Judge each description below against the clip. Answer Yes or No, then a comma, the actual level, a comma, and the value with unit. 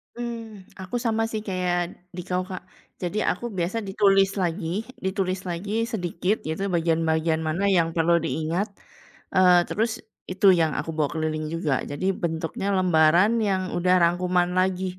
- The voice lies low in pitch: No, medium, 180 Hz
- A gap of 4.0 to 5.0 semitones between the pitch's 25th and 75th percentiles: No, average, 2.8 semitones